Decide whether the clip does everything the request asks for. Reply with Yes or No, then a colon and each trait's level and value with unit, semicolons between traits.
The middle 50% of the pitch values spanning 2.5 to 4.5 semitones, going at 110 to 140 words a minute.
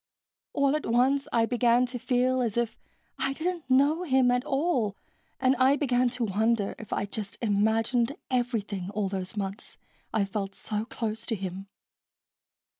No: average, 3.7 semitones; average, 160 wpm